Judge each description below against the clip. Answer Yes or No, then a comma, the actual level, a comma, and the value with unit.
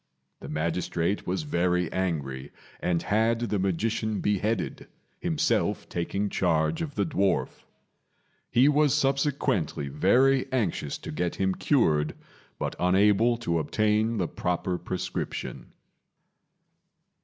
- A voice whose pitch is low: Yes, very low, 95 Hz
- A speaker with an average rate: No, slow, 110 wpm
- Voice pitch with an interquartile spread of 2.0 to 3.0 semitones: No, average, 5.2 semitones